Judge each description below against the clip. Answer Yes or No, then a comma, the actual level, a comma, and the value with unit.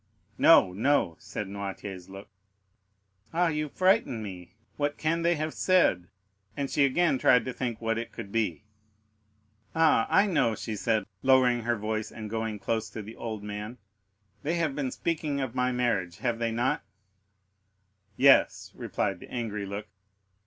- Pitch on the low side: Yes, low, 115 Hz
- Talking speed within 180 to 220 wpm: No, average, 155 wpm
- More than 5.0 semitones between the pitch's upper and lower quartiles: Yes, wide, 5.4 semitones